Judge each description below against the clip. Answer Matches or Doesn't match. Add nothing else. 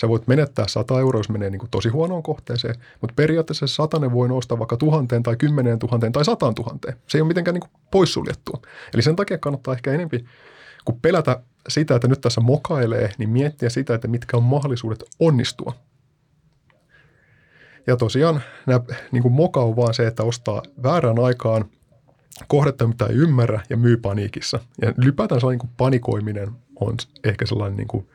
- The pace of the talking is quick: Matches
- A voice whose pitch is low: Matches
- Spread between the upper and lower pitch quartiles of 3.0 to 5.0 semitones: Matches